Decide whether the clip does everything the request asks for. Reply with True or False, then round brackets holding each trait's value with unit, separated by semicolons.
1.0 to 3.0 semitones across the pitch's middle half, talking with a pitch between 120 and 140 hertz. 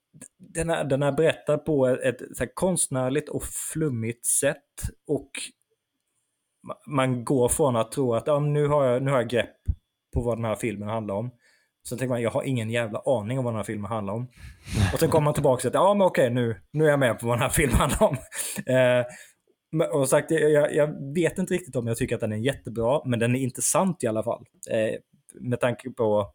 False (4.2 semitones; 125 Hz)